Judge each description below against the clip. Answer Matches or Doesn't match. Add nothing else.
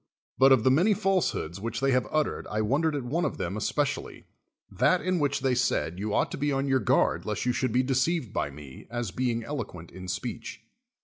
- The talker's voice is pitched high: Doesn't match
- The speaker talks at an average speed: Doesn't match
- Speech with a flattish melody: Doesn't match